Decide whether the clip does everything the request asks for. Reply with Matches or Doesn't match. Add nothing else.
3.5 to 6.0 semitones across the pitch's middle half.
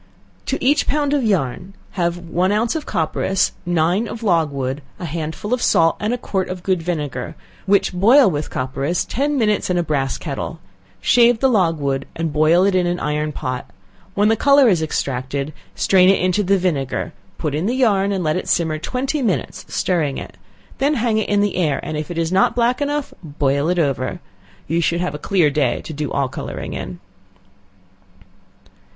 Matches